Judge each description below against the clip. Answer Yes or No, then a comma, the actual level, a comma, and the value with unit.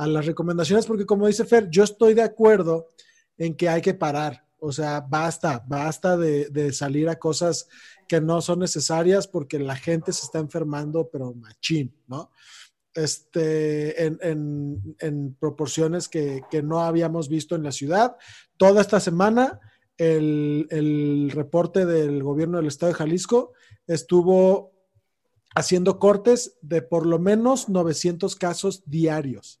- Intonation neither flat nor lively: Yes, average, 3.5 semitones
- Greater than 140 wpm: Yes, average, 150 wpm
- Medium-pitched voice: Yes, medium, 165 Hz